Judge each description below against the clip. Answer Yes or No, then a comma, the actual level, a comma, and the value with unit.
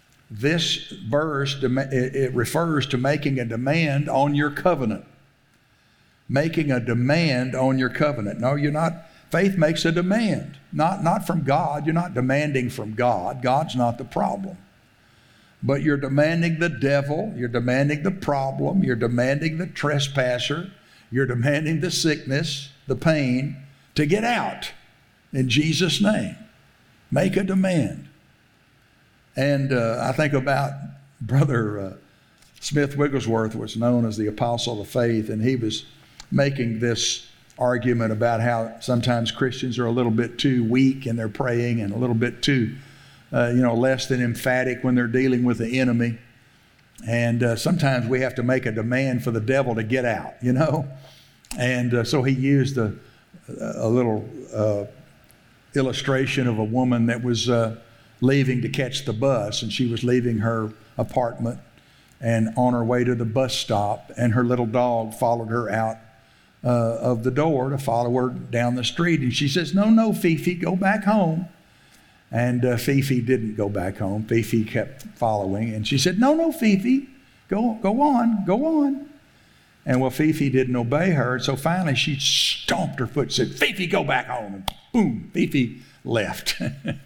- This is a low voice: Yes, low, 130 Hz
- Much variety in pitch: No, average, 3.8 semitones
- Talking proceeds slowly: No, average, 165 wpm